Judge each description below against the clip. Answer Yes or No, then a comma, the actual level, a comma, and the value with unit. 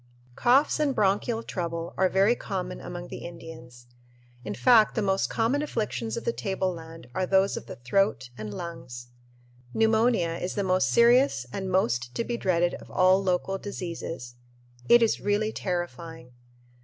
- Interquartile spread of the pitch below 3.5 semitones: No, average, 4.5 semitones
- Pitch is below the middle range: No, medium, 185 Hz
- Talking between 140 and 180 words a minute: Yes, average, 155 wpm